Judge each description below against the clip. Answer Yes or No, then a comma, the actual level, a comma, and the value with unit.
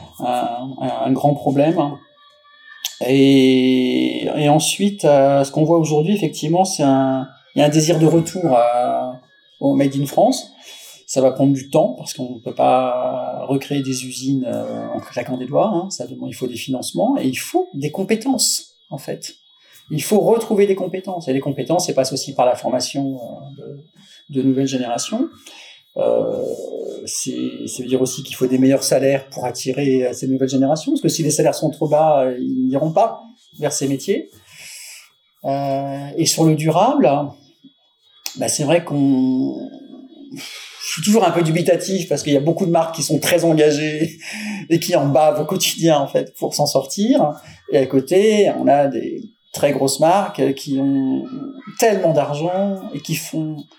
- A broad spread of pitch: Yes, wide, 6.0 semitones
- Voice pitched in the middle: Yes, medium, 150 Hz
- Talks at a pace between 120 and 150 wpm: No, average, 175 wpm